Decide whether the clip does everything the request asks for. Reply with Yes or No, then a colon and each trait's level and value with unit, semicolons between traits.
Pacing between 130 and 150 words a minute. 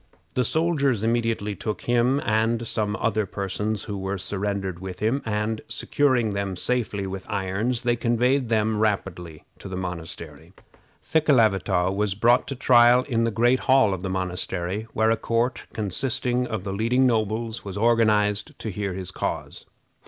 No: average, 160 wpm